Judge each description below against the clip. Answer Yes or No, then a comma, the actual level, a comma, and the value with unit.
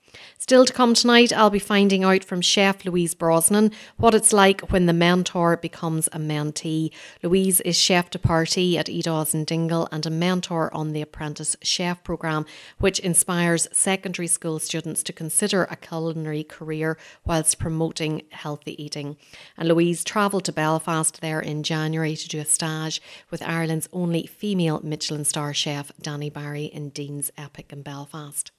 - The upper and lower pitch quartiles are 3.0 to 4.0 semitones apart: No, narrow, 2.6 semitones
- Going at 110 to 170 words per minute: Yes, average, 165 wpm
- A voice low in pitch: No, medium, 165 Hz